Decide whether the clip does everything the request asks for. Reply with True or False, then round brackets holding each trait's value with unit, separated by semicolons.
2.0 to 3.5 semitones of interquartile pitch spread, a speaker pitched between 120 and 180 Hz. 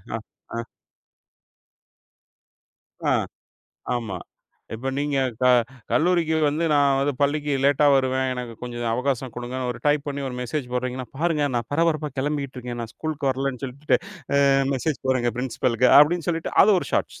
True (2.9 semitones; 135 Hz)